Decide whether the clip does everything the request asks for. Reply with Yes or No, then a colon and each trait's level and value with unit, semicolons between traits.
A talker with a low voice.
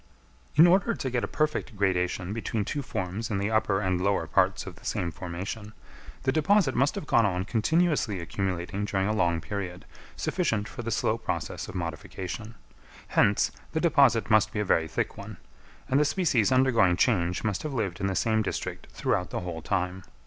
Yes: low, 105 Hz